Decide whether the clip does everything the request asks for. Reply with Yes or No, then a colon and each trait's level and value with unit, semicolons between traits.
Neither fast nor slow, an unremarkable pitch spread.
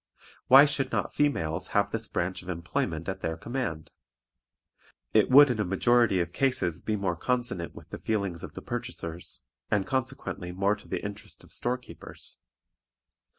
No: average, 165 wpm; wide, 6.0 semitones